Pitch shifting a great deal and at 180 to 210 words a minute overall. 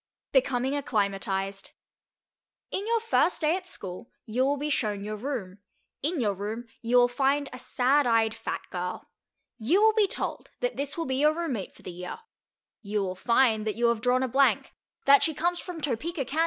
Yes: wide, 5.7 semitones; average, 195 wpm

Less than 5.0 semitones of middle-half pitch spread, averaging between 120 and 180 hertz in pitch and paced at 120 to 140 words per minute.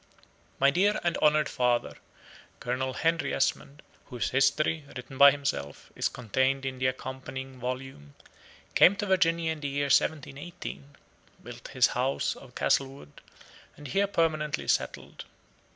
Yes: average, 3.4 semitones; medium, 140 Hz; slow, 135 wpm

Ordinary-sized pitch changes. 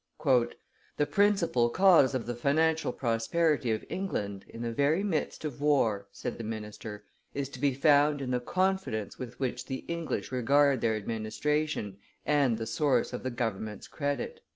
Yes: average, 4.8 semitones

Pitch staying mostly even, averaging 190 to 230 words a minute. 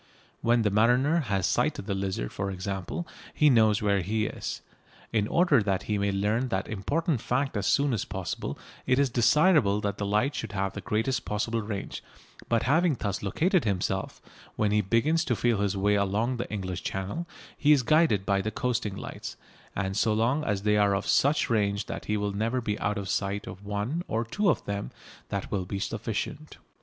No: average, 4.0 semitones; average, 200 wpm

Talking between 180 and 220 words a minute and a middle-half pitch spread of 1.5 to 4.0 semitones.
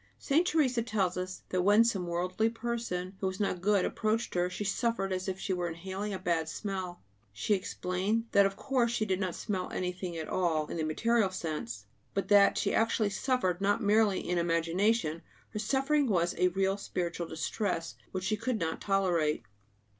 Yes: average, 185 wpm; average, 3.4 semitones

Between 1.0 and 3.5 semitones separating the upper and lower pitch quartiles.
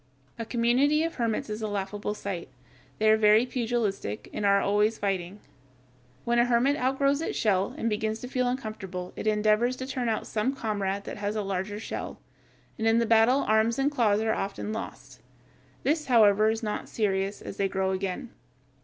Yes: average, 2.9 semitones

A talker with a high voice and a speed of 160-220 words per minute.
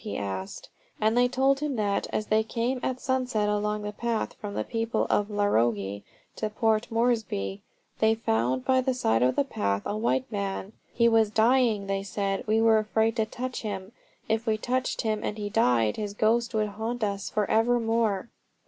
Yes: high, 215 Hz; average, 190 wpm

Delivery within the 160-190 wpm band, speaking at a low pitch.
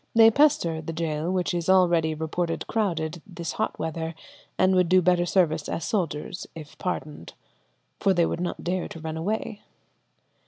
No: average, 165 wpm; medium, 170 Hz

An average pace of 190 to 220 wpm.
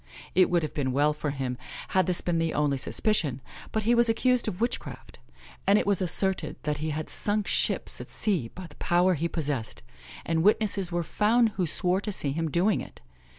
Yes: fast, 205 wpm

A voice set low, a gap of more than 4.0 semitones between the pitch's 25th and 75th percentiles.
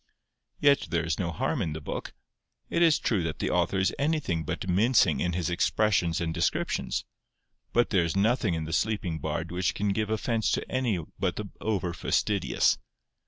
Yes: very low, 90 Hz; average, 4.9 semitones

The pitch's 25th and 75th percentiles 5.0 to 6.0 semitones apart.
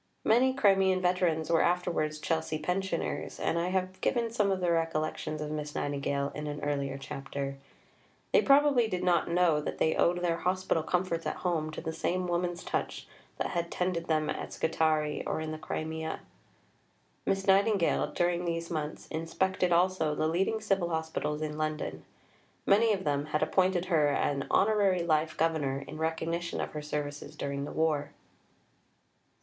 No: average, 3.1 semitones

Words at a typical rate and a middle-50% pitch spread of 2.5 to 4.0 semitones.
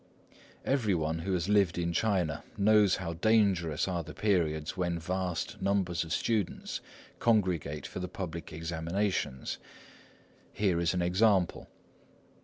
No: slow, 130 wpm; average, 3.1 semitones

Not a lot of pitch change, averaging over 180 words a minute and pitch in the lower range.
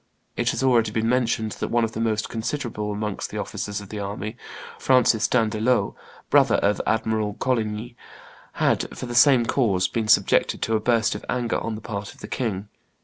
Yes: narrow, 2.1 semitones; average, 190 wpm; low, 110 Hz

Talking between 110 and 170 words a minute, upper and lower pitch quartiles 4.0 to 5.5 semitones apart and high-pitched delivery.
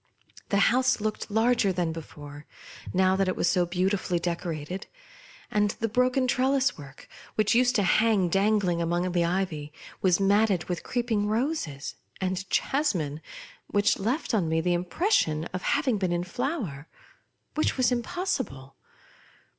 Yes: average, 150 wpm; average, 5.1 semitones; high, 195 Hz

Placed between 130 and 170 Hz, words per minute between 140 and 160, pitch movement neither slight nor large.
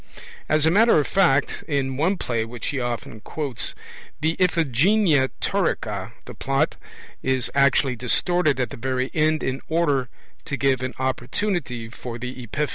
Yes: low, 135 Hz; average, 155 wpm; average, 4.0 semitones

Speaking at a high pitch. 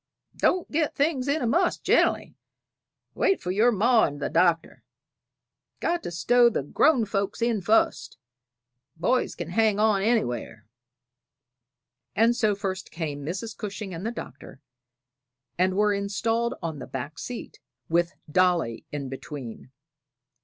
Yes: high, 200 Hz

